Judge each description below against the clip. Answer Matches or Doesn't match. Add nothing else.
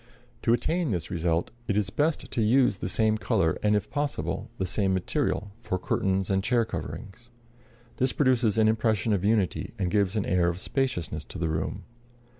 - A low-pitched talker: Matches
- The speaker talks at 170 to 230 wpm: Matches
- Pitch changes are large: Doesn't match